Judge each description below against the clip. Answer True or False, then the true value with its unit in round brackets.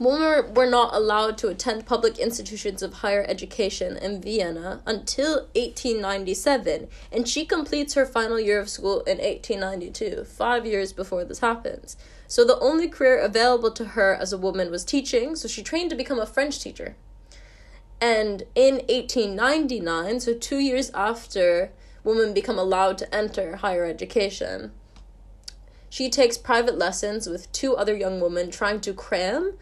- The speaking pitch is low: False (225 Hz)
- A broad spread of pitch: False (4.9 semitones)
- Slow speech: False (155 wpm)